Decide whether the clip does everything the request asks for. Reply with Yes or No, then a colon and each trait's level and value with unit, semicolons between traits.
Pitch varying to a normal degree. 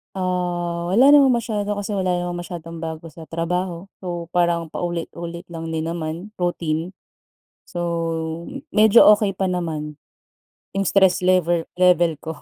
No: narrow, 1.8 semitones